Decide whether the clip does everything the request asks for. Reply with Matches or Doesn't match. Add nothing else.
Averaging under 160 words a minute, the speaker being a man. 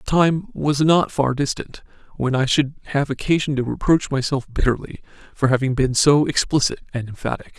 Doesn't match